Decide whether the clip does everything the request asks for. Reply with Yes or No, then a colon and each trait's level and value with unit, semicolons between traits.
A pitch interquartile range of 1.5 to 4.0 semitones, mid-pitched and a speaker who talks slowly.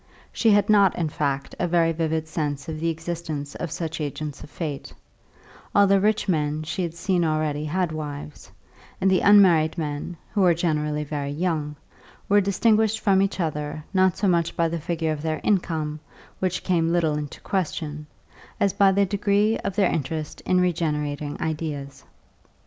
No: average, 3.7 semitones; medium, 165 Hz; average, 170 wpm